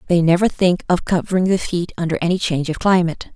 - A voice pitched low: No, medium, 175 Hz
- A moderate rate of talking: No, fast, 215 wpm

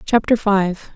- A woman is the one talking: Yes, female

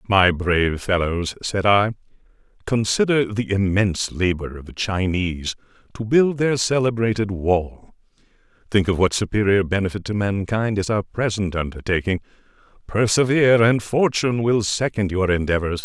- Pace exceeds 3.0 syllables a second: Yes, 4.9 syllables/s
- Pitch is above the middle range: No, low, 100 Hz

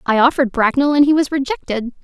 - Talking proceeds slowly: No, fast, 205 wpm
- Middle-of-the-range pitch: No, very high, 265 Hz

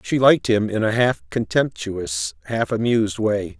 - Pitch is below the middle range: Yes, low, 115 Hz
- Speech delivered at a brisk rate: No, average, 165 wpm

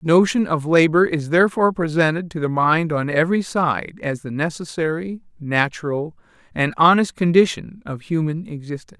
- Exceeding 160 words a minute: No, average, 155 wpm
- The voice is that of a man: Yes, male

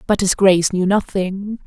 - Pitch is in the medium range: No, high, 195 Hz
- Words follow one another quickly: No, average, 180 wpm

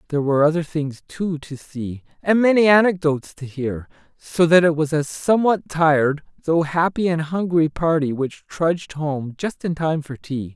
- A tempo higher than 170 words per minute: Yes, average, 180 wpm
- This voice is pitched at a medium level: Yes, medium, 160 Hz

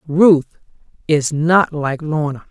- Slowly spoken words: Yes, slow, 120 wpm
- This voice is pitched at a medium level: Yes, medium, 155 Hz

